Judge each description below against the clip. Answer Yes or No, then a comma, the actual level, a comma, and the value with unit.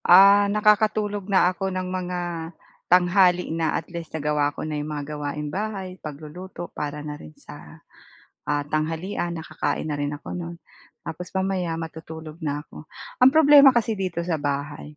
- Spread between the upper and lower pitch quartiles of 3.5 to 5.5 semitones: Yes, average, 4.2 semitones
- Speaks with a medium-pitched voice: Yes, medium, 170 Hz